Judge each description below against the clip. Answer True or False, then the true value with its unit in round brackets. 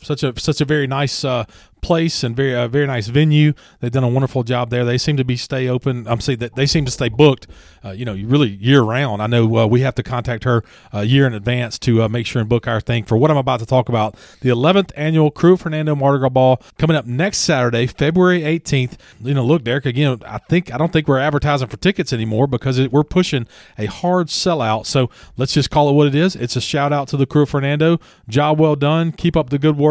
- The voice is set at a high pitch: False (135 Hz)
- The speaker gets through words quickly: True (255 wpm)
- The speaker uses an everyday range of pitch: True (3.8 semitones)